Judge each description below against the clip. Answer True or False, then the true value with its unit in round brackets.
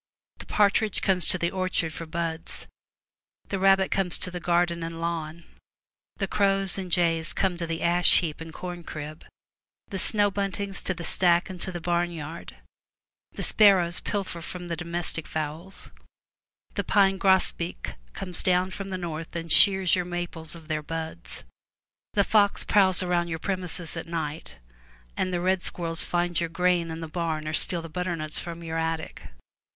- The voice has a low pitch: False (175 Hz)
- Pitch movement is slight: True (2.2 semitones)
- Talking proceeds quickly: False (175 wpm)